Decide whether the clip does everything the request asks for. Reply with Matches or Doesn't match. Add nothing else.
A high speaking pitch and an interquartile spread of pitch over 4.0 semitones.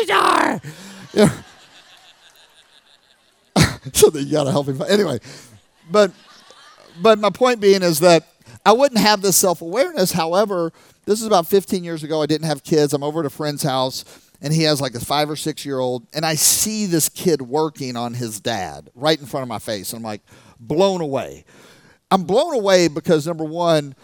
Doesn't match